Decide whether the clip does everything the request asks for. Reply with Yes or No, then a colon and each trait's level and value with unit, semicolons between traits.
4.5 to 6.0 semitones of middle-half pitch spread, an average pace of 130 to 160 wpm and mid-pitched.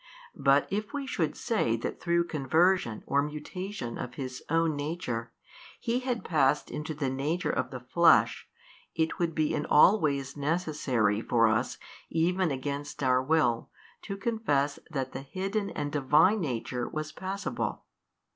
Yes: average, 5.1 semitones; average, 155 wpm; medium, 150 Hz